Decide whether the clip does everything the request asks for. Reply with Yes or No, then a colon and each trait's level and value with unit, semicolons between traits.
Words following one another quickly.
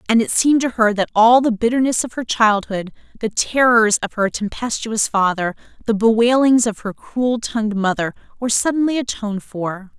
No: average, 175 wpm